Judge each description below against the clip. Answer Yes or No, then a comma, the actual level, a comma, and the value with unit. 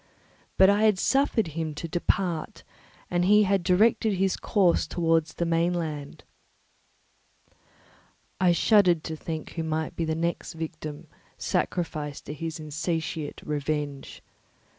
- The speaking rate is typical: No, slow, 125 wpm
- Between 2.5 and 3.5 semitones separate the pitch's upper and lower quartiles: Yes, average, 2.8 semitones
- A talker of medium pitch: Yes, medium, 165 Hz